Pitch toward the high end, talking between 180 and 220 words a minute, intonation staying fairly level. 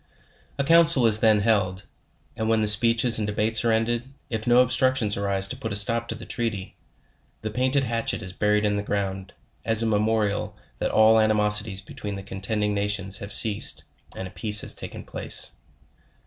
No: low, 110 Hz; average, 190 wpm; narrow, 2.2 semitones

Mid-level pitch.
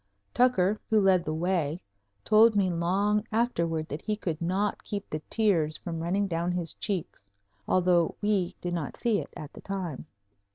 Yes: medium, 180 Hz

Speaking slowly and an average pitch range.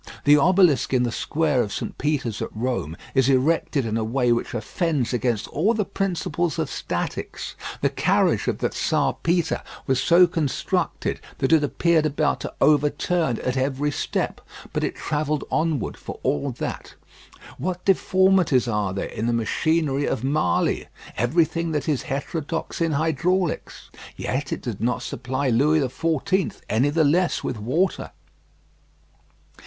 No: average, 150 wpm; average, 4.9 semitones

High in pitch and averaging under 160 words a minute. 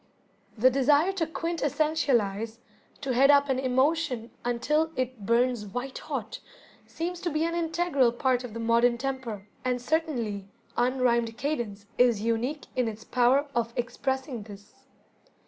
Yes: very high, 255 Hz; average, 140 wpm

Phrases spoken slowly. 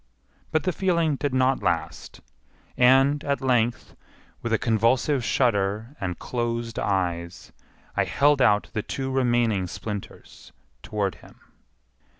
Yes: slow, 125 wpm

